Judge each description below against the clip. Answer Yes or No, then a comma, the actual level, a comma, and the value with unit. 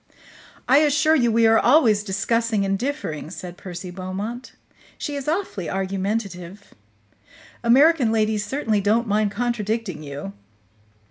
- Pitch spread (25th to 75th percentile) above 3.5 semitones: Yes, average, 3.9 semitones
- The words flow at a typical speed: No, slow, 125 wpm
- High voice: Yes, high, 215 Hz